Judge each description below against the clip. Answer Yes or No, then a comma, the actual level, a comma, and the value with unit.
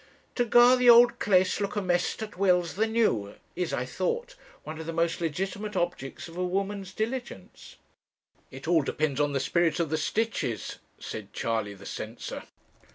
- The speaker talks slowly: No, average, 170 wpm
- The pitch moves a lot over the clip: Yes, wide, 5.8 semitones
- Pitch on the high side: No, medium, 180 Hz